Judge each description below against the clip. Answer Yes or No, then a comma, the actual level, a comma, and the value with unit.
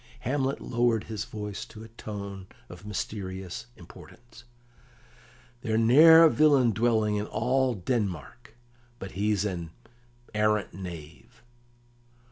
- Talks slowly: Yes, slow, 110 wpm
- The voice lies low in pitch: Yes, low, 105 Hz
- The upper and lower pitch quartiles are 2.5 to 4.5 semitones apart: Yes, average, 3.6 semitones